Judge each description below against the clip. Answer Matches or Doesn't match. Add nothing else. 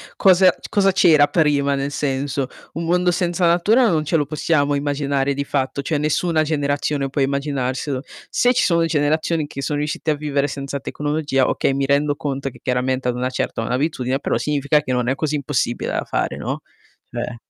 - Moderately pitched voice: Matches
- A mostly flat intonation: Matches